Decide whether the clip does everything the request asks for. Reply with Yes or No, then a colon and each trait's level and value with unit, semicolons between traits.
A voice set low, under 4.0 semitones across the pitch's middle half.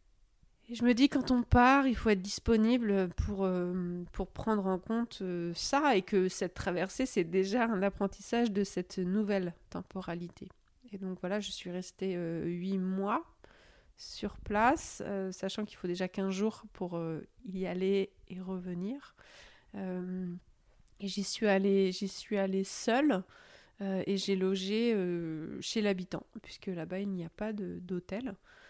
No: high, 195 Hz; average, 2.7 semitones